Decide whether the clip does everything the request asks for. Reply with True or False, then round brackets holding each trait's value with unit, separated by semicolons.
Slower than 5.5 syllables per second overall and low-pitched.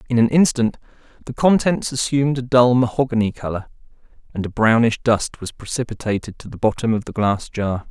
False (5.6 syllables/s; 115 Hz)